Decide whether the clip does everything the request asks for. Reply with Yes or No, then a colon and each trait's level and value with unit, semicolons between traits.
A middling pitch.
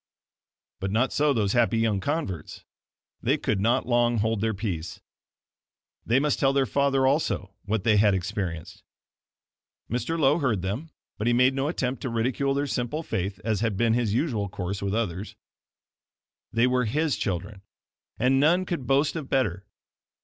No: low, 115 Hz